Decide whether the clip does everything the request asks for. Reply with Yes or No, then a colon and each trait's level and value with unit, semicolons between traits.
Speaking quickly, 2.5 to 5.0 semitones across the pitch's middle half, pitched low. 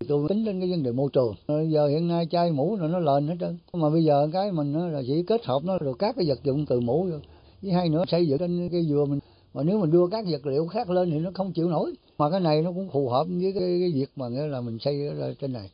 No: fast, 300 wpm; average, 3.9 semitones; medium, 160 Hz